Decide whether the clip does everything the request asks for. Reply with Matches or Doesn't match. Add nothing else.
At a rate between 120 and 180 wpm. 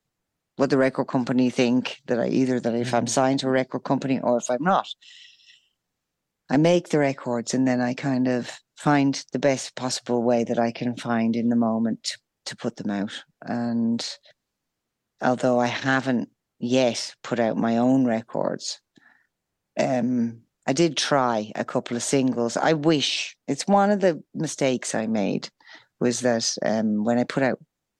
Matches